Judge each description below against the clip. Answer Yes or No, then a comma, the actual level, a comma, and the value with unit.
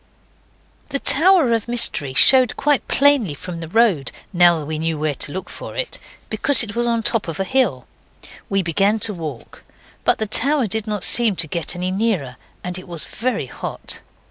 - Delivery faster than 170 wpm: Yes, average, 195 wpm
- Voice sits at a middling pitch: No, high, 200 Hz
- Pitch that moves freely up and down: Yes, wide, 6.3 semitones